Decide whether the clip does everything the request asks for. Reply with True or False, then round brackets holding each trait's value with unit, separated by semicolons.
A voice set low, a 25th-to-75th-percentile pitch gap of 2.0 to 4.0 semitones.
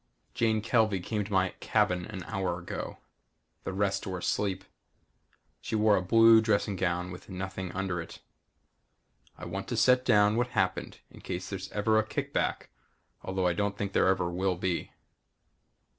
True (95 Hz; 2.7 semitones)